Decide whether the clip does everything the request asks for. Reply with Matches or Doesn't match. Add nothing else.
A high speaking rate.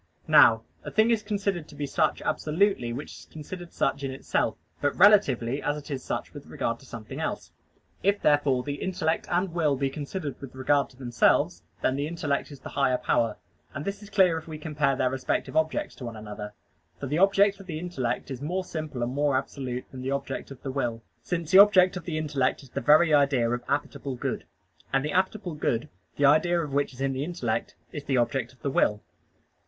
Matches